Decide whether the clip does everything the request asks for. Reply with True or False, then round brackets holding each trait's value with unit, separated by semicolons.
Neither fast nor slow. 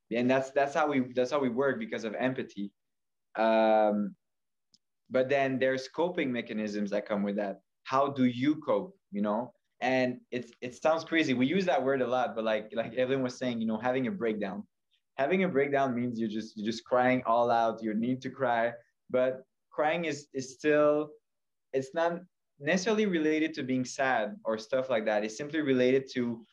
True (190 wpm)